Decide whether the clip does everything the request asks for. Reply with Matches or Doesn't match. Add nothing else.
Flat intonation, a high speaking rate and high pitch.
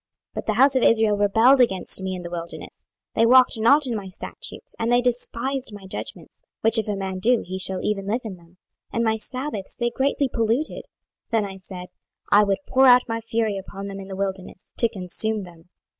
Doesn't match